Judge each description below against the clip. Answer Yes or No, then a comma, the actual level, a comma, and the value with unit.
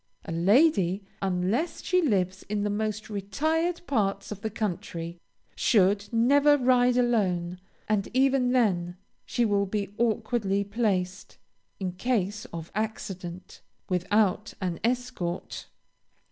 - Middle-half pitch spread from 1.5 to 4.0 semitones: No, average, 4.6 semitones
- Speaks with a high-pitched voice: Yes, high, 205 Hz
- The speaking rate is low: Yes, slow, 120 wpm